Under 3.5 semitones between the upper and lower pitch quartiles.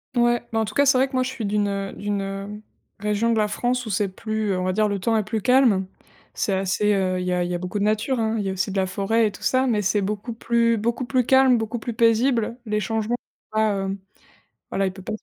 Yes: average, 3.0 semitones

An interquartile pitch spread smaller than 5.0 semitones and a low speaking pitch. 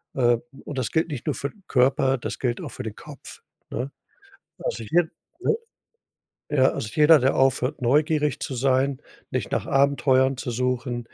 Yes: narrow, 2.5 semitones; low, 130 Hz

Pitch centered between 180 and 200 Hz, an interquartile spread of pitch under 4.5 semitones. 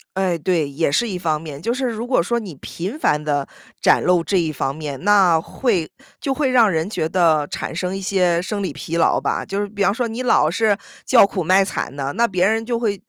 No: medium, 185 Hz; average, 5.3 semitones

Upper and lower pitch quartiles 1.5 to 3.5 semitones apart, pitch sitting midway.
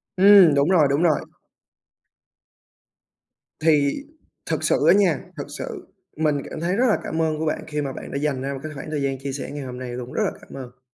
Yes: average, 2.8 semitones; medium, 150 Hz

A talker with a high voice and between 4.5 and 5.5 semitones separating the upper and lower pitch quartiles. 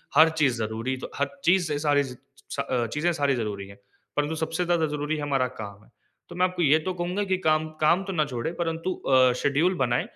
No: medium, 150 Hz; average, 4.9 semitones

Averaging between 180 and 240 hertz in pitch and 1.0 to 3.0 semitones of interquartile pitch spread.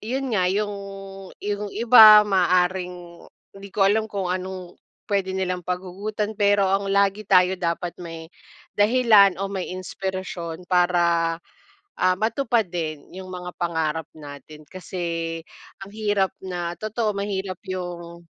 Yes: medium, 185 Hz; narrow, 2.5 semitones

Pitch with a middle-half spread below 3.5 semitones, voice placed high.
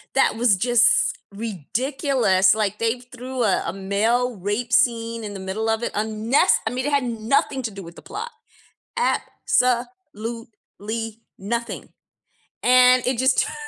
Yes: average, 2.9 semitones; high, 230 Hz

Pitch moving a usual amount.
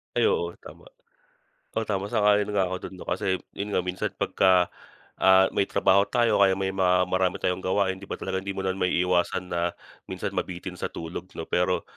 No: narrow, 1.5 semitones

